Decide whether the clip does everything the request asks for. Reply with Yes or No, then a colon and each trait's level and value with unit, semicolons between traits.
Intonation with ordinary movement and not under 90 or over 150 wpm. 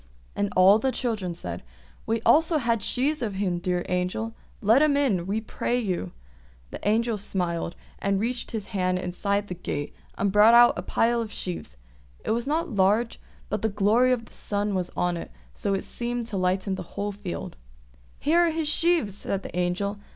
No: average, 4.3 semitones; average, 195 wpm